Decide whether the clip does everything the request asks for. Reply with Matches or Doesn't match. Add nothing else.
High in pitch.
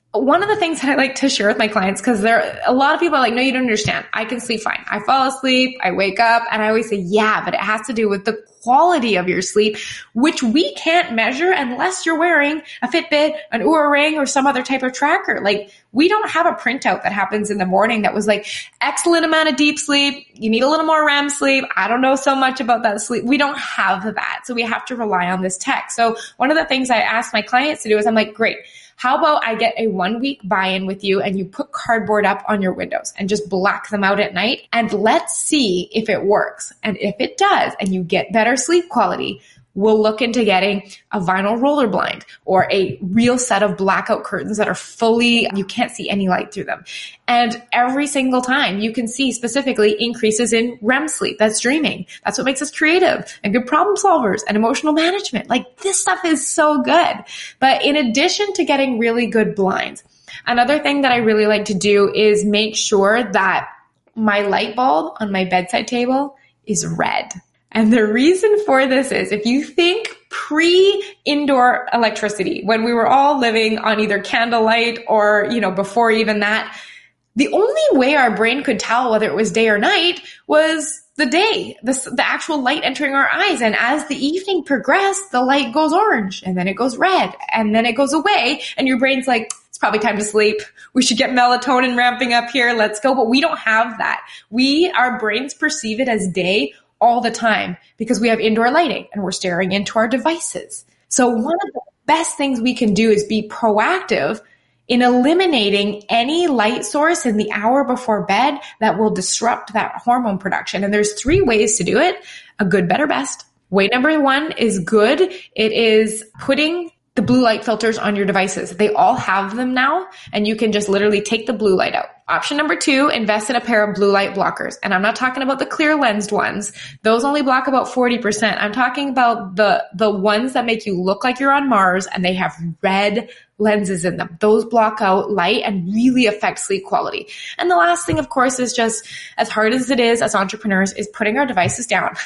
Matches